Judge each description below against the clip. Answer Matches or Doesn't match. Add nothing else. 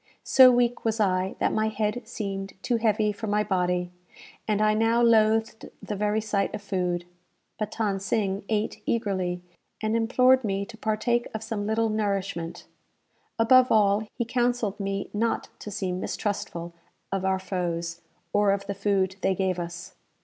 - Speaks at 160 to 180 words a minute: Matches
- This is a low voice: Doesn't match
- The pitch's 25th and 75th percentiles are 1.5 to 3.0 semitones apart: Matches